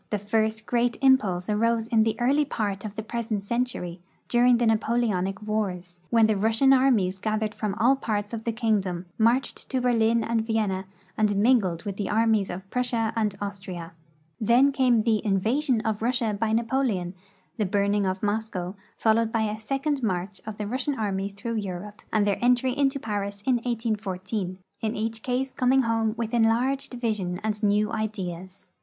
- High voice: Yes, high, 220 Hz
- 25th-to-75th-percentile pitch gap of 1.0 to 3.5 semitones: Yes, average, 2.8 semitones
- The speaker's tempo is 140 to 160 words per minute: No, average, 175 wpm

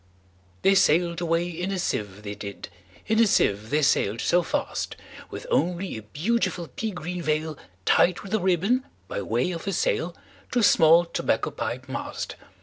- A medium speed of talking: Yes, average, 155 wpm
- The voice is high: No, medium, 175 Hz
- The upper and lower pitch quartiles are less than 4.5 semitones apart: No, average, 4.8 semitones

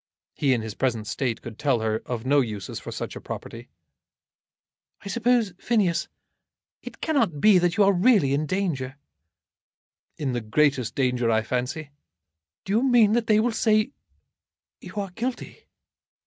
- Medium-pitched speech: Yes, medium, 150 Hz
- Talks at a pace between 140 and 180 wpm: Yes, average, 160 wpm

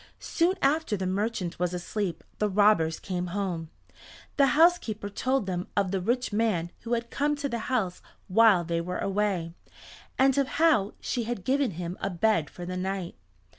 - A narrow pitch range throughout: No, average, 5.1 semitones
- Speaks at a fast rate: No, average, 175 wpm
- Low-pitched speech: No, high, 205 Hz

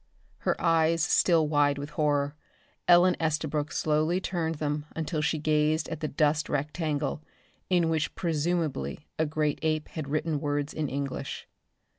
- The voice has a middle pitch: Yes, medium, 155 Hz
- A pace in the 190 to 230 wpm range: No, average, 145 wpm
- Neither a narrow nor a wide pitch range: No, narrow, 1.7 semitones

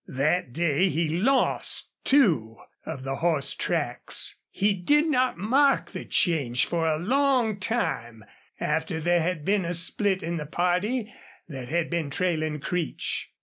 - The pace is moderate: Yes, average, 150 wpm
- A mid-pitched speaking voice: Yes, medium, 175 Hz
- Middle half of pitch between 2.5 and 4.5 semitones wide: No, average, 5.2 semitones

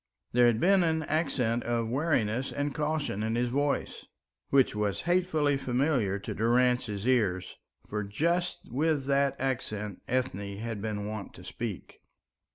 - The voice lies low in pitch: Yes, low, 125 Hz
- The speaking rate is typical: Yes, average, 145 wpm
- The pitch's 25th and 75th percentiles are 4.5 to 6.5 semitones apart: Yes, average, 5.2 semitones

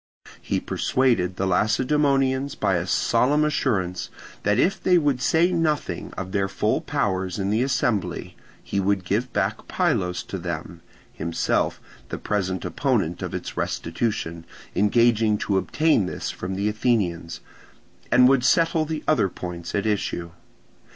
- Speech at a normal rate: Yes, average, 145 wpm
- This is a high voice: No, low, 105 Hz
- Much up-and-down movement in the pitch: Yes, wide, 6.2 semitones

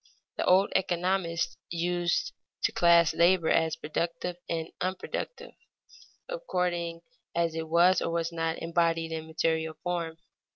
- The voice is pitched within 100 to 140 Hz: No, medium, 170 Hz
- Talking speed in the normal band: No, slow, 125 wpm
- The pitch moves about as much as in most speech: No, narrow, 1.5 semitones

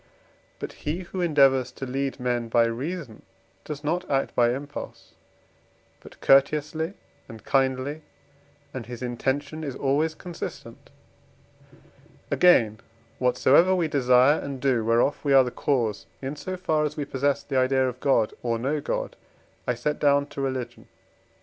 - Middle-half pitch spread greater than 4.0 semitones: No, average, 3.1 semitones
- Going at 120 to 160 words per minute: Yes, average, 150 wpm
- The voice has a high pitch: No, low, 135 Hz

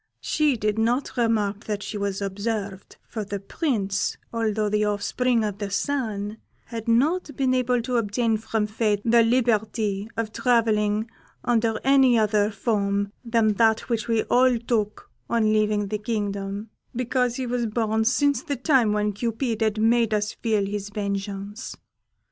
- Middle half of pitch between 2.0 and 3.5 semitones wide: Yes, narrow, 2.4 semitones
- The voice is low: No, high, 220 Hz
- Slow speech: No, average, 155 wpm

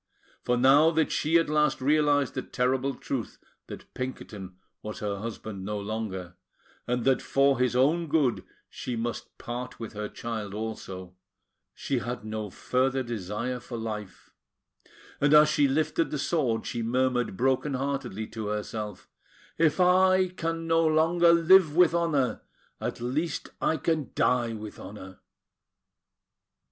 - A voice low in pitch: Yes, low, 125 Hz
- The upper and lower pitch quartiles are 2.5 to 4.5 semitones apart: No, wide, 5.6 semitones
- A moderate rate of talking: Yes, average, 145 wpm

